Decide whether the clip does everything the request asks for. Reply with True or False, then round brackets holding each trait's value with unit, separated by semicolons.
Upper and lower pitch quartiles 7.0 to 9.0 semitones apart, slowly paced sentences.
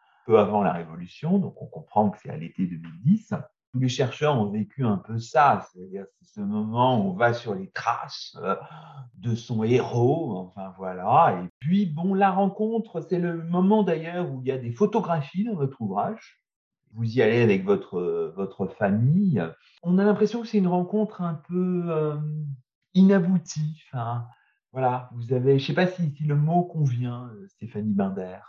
False (7.9 semitones; 185 wpm)